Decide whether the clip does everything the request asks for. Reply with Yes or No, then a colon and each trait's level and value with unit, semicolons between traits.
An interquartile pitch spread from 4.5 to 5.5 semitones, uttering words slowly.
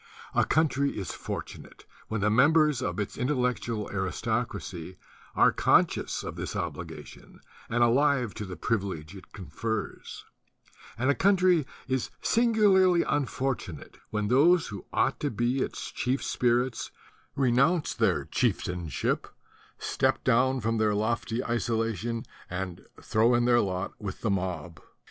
Yes: average, 4.8 semitones; slow, 130 wpm